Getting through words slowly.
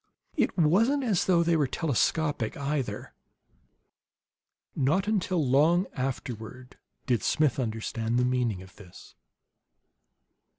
Yes: slow, 110 wpm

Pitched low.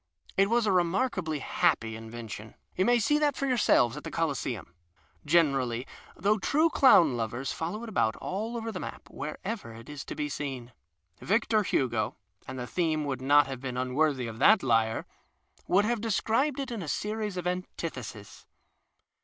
No: medium, 160 Hz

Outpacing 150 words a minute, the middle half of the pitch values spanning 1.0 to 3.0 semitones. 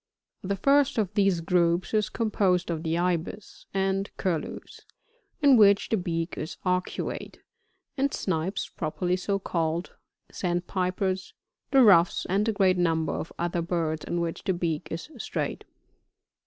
No: average, 145 wpm; average, 2.7 semitones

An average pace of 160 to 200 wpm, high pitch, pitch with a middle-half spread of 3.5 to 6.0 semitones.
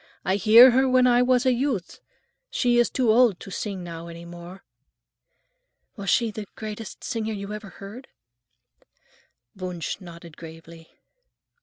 No: average, 145 wpm; high, 210 Hz; wide, 5.6 semitones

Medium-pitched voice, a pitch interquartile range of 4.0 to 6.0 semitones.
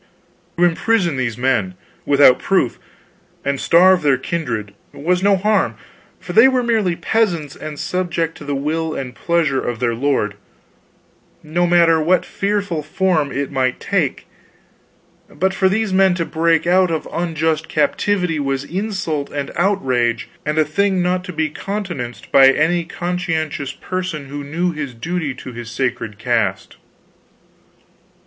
Yes: medium, 160 Hz; average, 4.9 semitones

